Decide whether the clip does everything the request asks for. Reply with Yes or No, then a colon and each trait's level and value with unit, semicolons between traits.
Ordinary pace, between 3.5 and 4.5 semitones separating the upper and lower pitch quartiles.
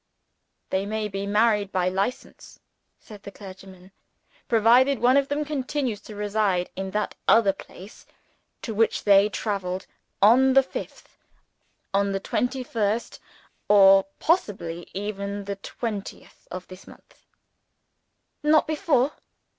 No: slow, 125 wpm; average, 3.8 semitones